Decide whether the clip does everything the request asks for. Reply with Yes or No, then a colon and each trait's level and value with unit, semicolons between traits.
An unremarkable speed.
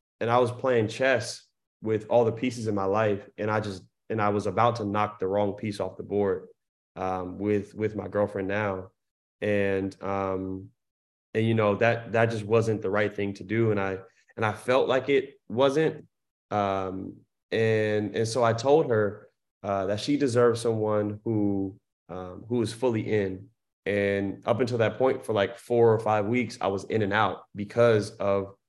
Yes: average, 190 wpm